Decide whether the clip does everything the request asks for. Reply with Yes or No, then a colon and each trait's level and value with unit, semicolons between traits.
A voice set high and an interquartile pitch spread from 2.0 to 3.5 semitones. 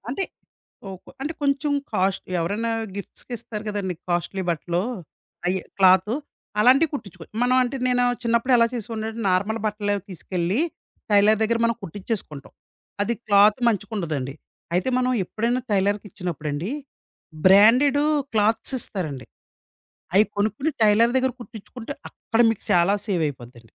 No: high, 210 Hz; average, 4.1 semitones